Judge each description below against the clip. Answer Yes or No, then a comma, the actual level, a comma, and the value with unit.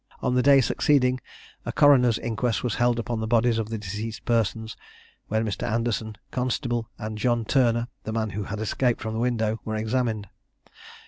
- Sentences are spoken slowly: No, average, 180 wpm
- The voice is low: Yes, low, 115 Hz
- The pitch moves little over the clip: Yes, narrow, 2.0 semitones